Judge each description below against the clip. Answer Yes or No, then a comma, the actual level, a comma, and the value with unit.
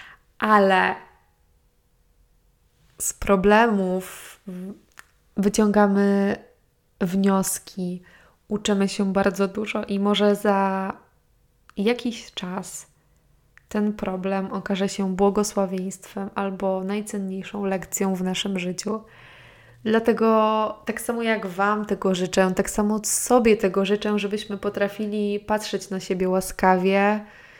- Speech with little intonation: Yes, narrow, 1.7 semitones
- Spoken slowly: Yes, slow, 95 wpm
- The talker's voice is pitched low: No, high, 200 Hz